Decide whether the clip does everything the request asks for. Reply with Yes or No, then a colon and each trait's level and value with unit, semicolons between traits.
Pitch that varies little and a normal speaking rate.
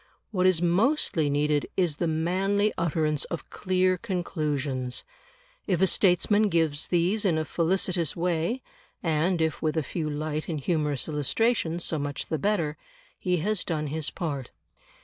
No: average, 3.4 semitones; average, 150 wpm